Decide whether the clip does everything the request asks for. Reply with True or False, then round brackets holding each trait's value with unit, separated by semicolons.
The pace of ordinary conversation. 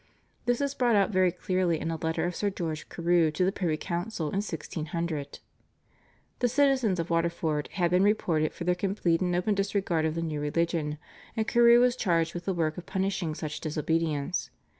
True (190 wpm)